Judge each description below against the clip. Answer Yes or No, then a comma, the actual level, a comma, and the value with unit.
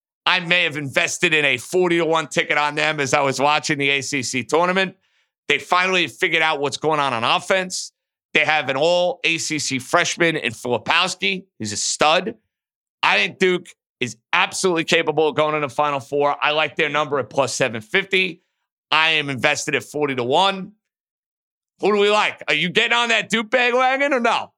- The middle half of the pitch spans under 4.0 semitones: No, average, 4.5 semitones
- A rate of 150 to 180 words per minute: No, average, 195 wpm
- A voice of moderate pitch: Yes, medium, 155 Hz